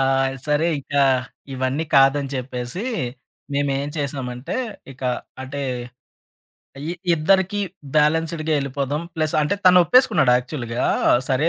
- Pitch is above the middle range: No, medium, 140 Hz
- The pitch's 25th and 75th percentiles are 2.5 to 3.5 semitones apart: Yes, average, 2.8 semitones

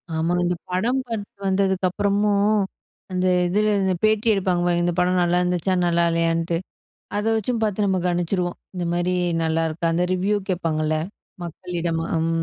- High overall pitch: No, medium, 180 Hz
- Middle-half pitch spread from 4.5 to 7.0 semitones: No, average, 2.8 semitones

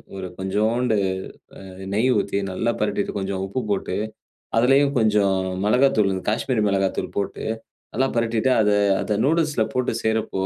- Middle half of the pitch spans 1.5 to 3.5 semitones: No, average, 4.0 semitones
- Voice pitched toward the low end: Yes, low, 110 Hz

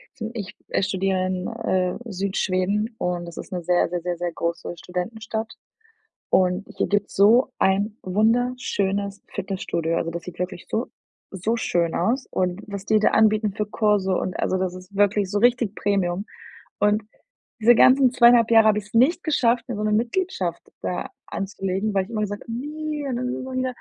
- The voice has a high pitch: Yes, high, 205 Hz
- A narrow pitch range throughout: No, average, 3.6 semitones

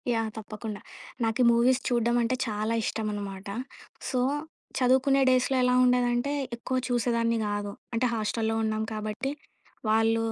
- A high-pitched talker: Yes, high, 230 Hz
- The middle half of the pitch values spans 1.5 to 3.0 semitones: Yes, narrow, 2.5 semitones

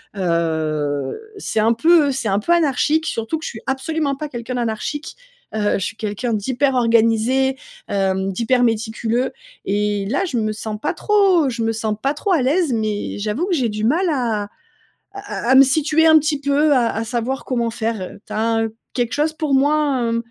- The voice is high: Yes, high, 240 Hz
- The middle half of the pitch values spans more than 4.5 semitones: Yes, average, 5.0 semitones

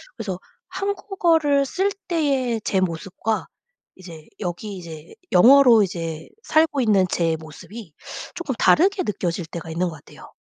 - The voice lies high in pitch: Yes, high, 210 Hz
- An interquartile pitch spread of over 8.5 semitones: Yes, wide, 8.9 semitones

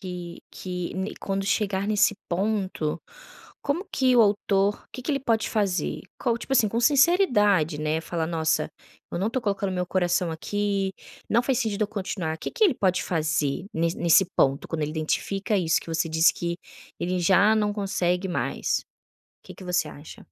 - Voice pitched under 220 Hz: Yes, high, 190 Hz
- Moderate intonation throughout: Yes, average, 3.7 semitones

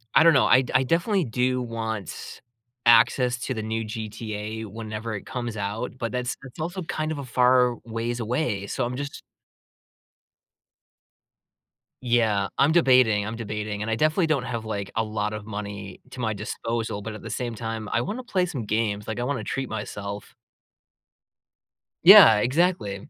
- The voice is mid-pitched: No, low, 115 Hz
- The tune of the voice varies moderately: Yes, average, 3.2 semitones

